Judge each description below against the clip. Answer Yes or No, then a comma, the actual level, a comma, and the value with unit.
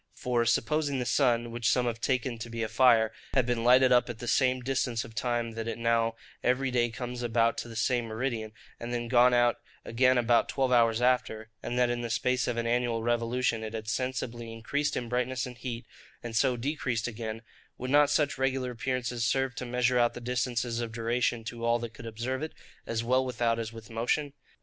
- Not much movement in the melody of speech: Yes, narrow, 1.7 semitones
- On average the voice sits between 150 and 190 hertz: No, low, 120 Hz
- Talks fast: Yes, fast, 210 wpm